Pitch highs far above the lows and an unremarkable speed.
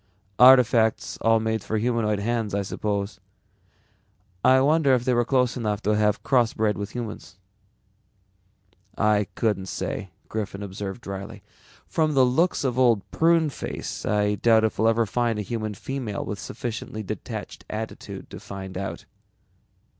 No: average, 3.0 semitones; average, 145 wpm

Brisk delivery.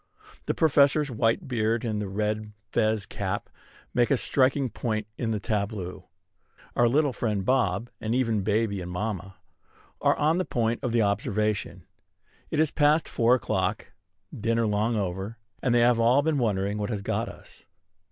No: average, 160 wpm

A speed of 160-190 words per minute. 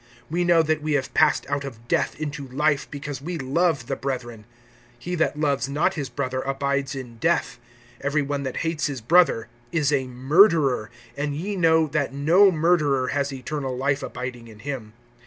Yes: average, 180 wpm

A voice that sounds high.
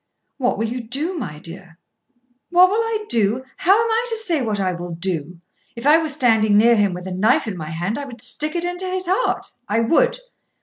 Yes: high, 240 Hz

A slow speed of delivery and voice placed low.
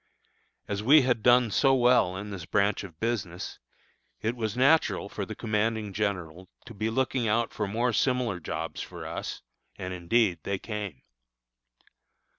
No: average, 155 wpm; low, 105 Hz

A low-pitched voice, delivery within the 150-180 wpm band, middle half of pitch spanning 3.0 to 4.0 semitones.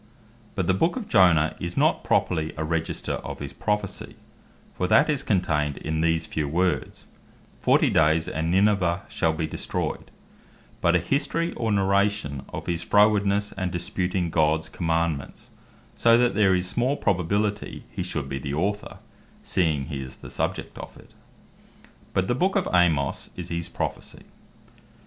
No: very low, 90 Hz; average, 160 wpm; average, 4.4 semitones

